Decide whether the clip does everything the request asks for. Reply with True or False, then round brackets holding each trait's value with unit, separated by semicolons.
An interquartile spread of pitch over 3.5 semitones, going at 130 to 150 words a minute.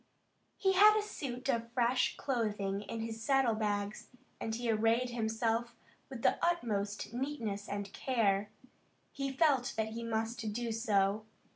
False (2.9 semitones; 145 wpm)